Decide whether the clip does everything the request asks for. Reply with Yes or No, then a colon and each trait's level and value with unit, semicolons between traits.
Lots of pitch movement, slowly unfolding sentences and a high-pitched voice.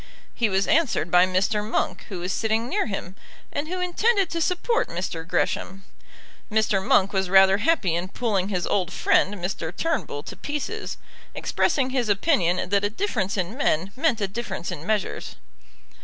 No: wide, 6.1 semitones; average, 170 wpm; high, 205 Hz